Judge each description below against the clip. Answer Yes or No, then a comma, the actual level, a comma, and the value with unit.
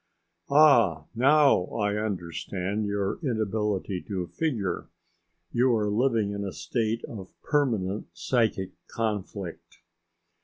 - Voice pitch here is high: No, low, 105 Hz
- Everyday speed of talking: No, slow, 105 wpm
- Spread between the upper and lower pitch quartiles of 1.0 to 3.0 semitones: No, average, 3.5 semitones